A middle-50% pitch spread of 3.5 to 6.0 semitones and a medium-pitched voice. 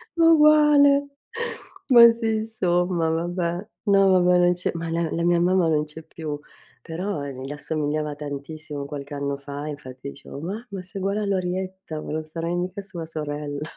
Yes: average, 4.4 semitones; medium, 170 Hz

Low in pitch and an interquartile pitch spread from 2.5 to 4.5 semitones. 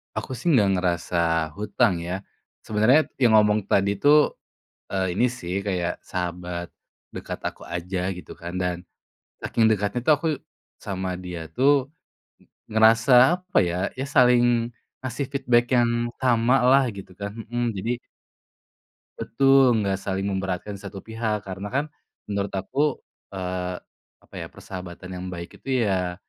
No: low, 105 Hz; average, 4.9 semitones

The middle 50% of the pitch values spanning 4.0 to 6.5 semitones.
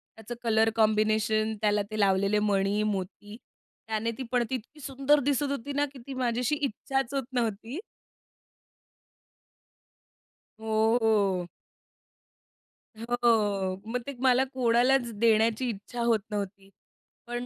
No: average, 3.2 semitones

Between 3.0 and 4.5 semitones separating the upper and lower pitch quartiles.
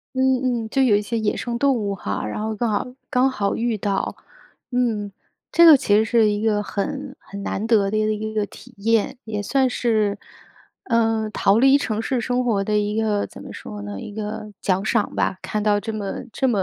No: narrow, 2.6 semitones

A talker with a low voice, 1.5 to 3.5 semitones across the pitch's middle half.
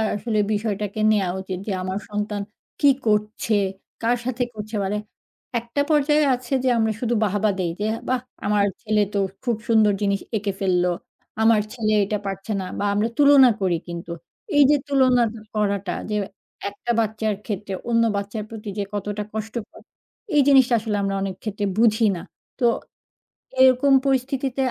No: high, 215 Hz; average, 3.1 semitones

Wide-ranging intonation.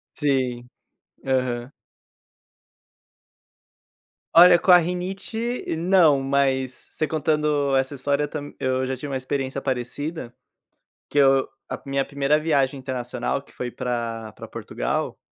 No: average, 2.7 semitones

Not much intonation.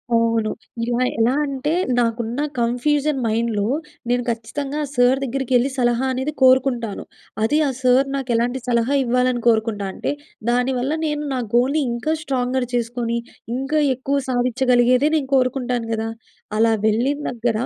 Yes: narrow, 2.3 semitones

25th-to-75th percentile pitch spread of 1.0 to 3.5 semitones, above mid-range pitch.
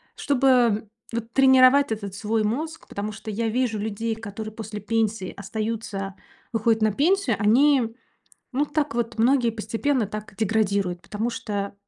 Yes: average, 3.1 semitones; high, 225 Hz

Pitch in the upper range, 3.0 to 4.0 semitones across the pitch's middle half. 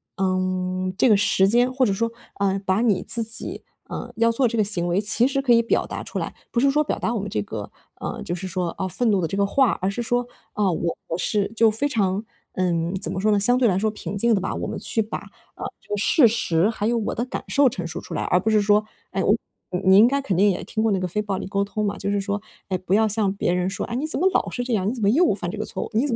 Yes: high, 205 Hz; average, 3.6 semitones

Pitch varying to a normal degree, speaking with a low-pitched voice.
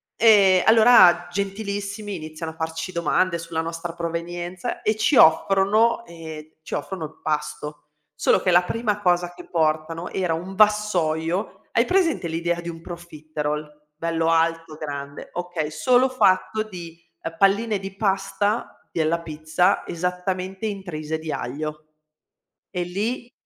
No: average, 3.5 semitones; medium, 175 Hz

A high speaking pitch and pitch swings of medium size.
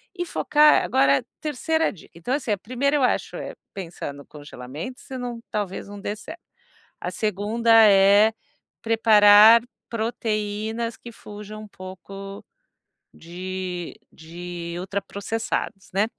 Yes: high, 205 Hz; average, 3.7 semitones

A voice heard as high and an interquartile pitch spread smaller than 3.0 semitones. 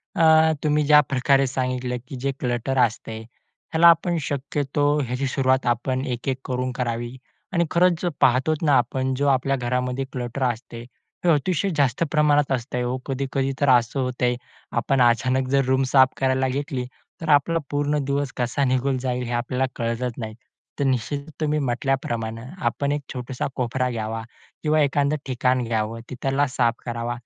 No: low, 130 Hz; narrow, 2.5 semitones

